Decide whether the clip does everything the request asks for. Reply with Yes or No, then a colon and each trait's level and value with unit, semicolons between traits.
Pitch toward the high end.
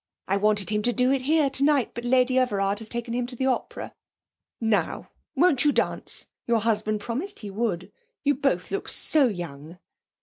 Yes: high, 235 Hz